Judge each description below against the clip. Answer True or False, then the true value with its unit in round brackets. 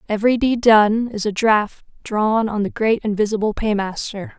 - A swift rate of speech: False (165 wpm)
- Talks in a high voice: True (215 Hz)